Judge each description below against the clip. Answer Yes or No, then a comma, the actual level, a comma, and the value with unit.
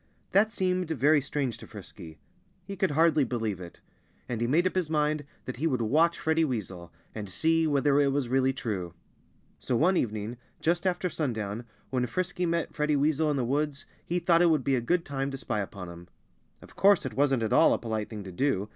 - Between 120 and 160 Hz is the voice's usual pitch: Yes, medium, 140 Hz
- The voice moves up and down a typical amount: No, wide, 6.0 semitones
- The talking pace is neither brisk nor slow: No, fast, 215 wpm